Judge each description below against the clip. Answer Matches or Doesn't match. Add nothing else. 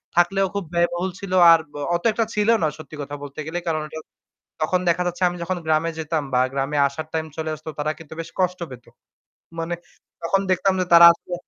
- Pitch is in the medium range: Matches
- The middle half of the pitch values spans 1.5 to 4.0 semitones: Matches